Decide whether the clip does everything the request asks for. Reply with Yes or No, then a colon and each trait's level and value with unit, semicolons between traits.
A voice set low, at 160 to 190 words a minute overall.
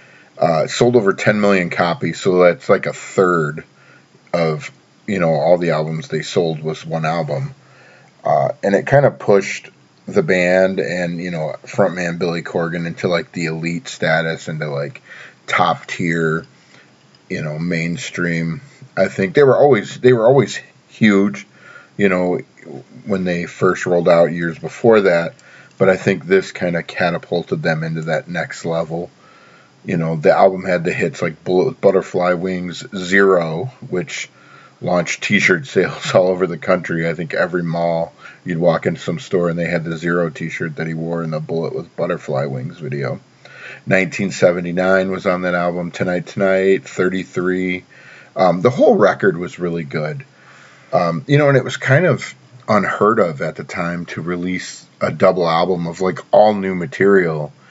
Yes: very low, 90 Hz; average, 170 wpm